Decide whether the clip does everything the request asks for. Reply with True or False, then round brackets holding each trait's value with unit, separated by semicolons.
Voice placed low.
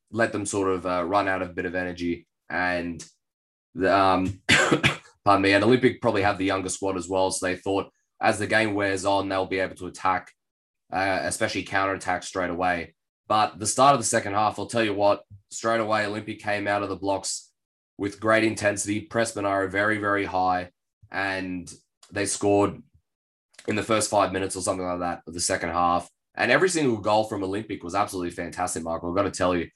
True (95 Hz)